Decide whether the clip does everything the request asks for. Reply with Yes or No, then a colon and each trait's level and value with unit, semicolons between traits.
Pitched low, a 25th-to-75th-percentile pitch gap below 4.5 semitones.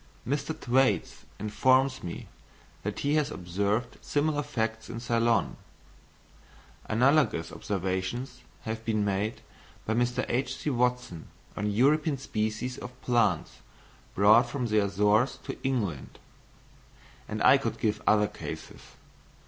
Yes: low, 115 Hz; average, 3.8 semitones